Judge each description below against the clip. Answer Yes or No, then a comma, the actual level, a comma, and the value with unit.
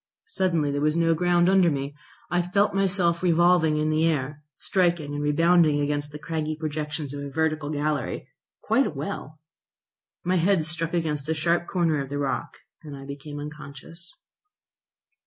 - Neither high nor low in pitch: Yes, medium, 155 Hz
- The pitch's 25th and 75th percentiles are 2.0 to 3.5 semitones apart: Yes, average, 2.8 semitones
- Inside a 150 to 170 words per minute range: Yes, average, 160 wpm